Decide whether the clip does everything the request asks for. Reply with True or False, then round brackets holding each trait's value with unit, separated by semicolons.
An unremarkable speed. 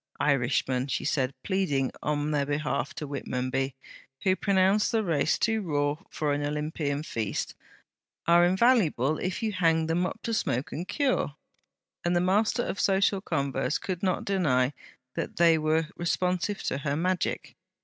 True (155 wpm)